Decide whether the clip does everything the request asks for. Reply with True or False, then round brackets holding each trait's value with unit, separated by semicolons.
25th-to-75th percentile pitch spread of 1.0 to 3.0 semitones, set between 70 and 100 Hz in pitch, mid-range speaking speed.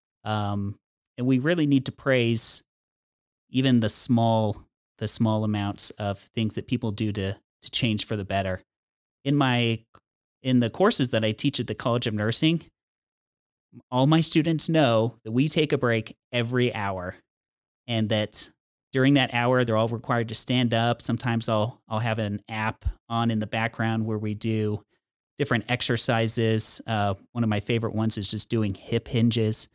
False (2.6 semitones; 115 Hz; 170 wpm)